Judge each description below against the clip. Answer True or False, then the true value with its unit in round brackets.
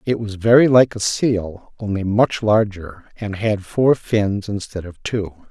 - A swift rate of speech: False (175 wpm)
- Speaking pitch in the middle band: False (105 Hz)